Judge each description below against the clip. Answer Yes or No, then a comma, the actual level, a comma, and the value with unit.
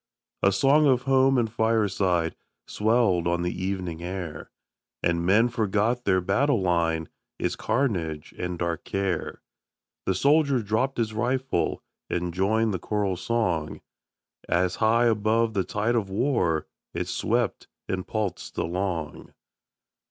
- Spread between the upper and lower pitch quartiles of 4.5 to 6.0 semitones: Yes, average, 4.8 semitones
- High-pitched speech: No, low, 100 Hz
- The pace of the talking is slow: Yes, slow, 130 wpm